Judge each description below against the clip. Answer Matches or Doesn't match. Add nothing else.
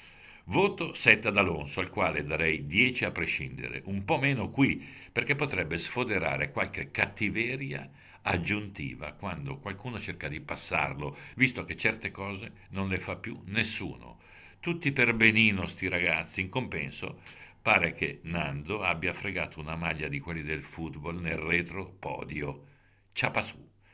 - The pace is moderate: Matches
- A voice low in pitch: Matches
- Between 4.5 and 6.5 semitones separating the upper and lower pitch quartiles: Matches